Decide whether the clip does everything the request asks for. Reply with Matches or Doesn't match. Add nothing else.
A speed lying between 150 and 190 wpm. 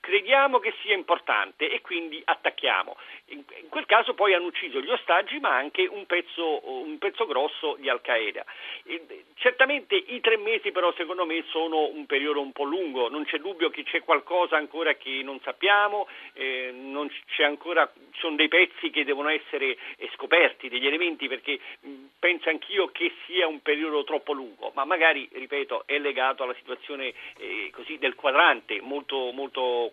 Matches